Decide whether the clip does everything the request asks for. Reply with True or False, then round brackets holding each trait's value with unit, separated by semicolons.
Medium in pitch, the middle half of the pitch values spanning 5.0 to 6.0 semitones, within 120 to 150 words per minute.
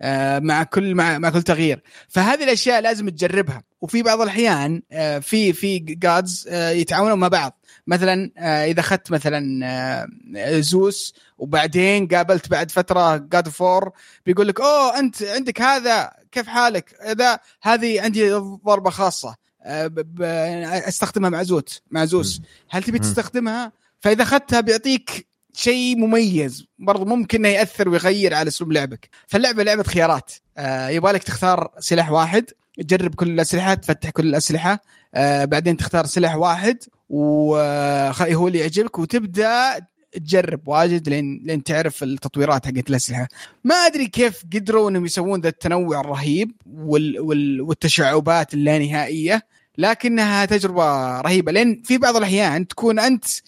True (180 Hz; 5.3 semitones; 125 wpm)